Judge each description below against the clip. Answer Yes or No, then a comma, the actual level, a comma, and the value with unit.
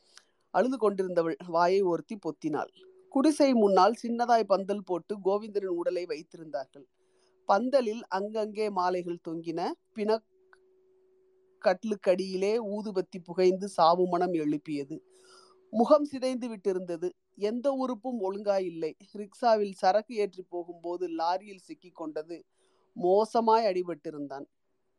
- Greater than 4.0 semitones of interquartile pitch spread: Yes, average, 5.2 semitones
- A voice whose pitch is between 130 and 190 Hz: No, high, 200 Hz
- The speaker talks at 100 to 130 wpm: No, average, 90 wpm